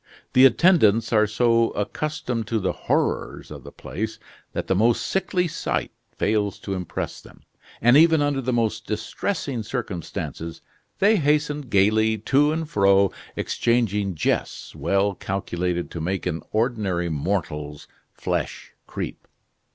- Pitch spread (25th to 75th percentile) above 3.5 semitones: Yes, average, 5.2 semitones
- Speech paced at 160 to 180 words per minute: No, slow, 135 wpm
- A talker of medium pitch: No, low, 110 Hz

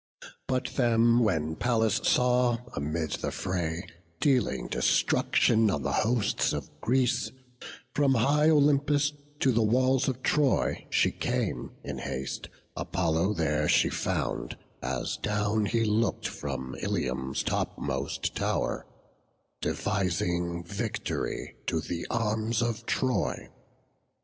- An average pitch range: No, wide, 6.5 semitones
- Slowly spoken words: Yes, slow, 115 wpm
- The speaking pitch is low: Yes, low, 110 Hz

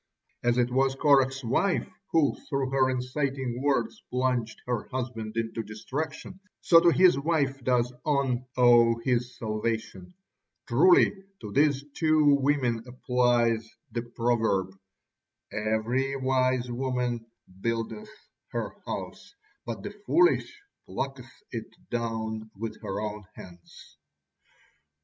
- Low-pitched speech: Yes, low, 125 Hz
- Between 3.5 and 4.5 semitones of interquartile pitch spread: No, average, 3.1 semitones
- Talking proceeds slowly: Yes, slow, 115 wpm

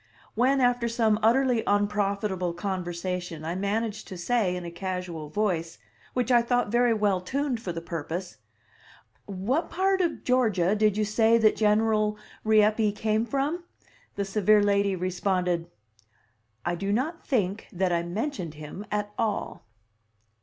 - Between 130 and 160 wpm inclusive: Yes, average, 145 wpm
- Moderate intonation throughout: Yes, average, 4.0 semitones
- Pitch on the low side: No, high, 210 Hz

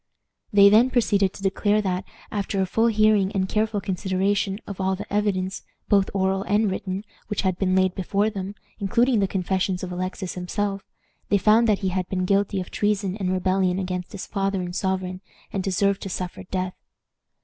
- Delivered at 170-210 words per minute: Yes, average, 185 wpm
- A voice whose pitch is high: Yes, high, 195 Hz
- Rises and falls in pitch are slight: Yes, narrow, 1.6 semitones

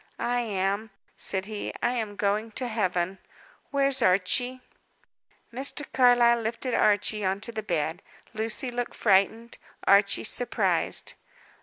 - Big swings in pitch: No, average, 3.5 semitones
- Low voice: No, high, 220 Hz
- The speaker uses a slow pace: Yes, slow, 125 wpm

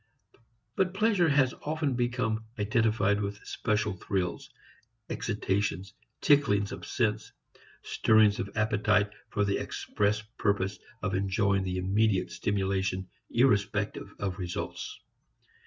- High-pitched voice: No, low, 105 Hz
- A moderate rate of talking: No, slow, 105 wpm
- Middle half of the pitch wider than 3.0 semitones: No, narrow, 2.4 semitones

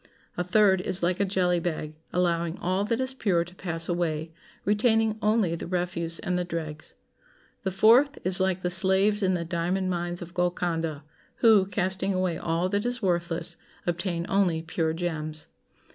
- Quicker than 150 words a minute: Yes, average, 170 wpm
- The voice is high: No, medium, 180 Hz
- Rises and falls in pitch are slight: Yes, narrow, 2.3 semitones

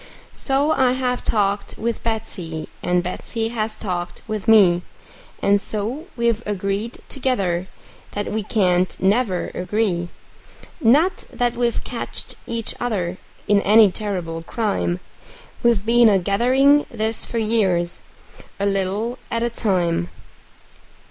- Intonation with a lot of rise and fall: No, average, 4.0 semitones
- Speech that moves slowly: Yes, slow, 125 wpm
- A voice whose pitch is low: No, high, 215 Hz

